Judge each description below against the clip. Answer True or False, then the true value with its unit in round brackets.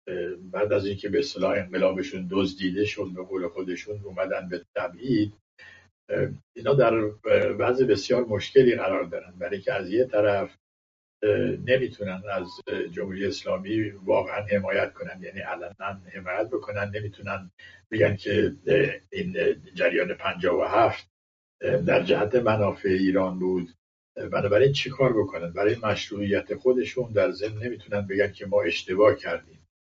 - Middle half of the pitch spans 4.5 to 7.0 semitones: False (2.6 semitones)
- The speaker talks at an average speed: False (130 wpm)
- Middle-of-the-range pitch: False (100 Hz)